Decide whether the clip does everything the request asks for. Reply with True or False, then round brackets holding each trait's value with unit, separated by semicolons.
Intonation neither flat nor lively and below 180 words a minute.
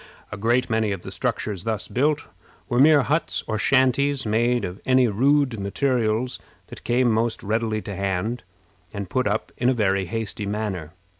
True (3.8 semitones; 170 wpm)